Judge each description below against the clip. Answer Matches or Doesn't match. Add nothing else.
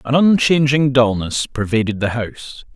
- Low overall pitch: Matches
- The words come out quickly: Doesn't match